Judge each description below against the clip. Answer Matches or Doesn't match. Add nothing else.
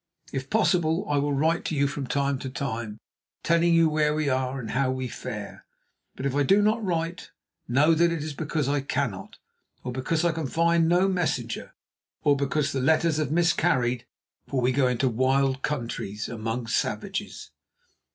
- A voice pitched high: Doesn't match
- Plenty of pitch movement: Doesn't match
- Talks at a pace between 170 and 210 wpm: Matches